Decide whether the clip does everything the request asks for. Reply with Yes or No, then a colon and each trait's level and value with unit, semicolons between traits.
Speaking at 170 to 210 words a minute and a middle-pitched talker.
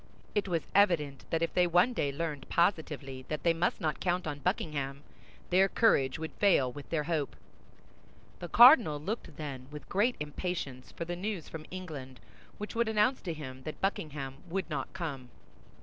Yes: average, 175 wpm; medium, 160 Hz